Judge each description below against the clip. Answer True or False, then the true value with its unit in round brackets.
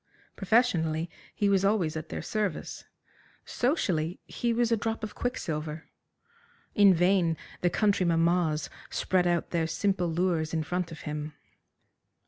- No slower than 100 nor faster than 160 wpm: True (135 wpm)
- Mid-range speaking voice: True (175 Hz)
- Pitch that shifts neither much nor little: True (4.0 semitones)